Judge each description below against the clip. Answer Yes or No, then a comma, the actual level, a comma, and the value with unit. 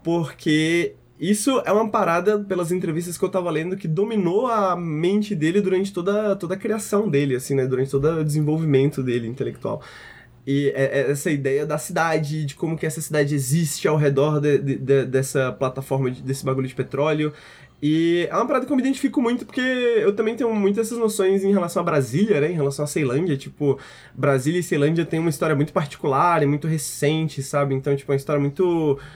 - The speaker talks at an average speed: No, fast, 205 wpm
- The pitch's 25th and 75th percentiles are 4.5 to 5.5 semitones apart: Yes, average, 5.1 semitones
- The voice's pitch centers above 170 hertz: No, medium, 155 Hz